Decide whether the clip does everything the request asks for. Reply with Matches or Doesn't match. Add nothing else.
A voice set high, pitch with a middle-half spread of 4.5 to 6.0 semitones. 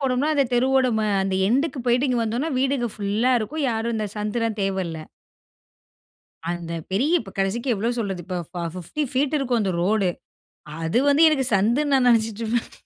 Matches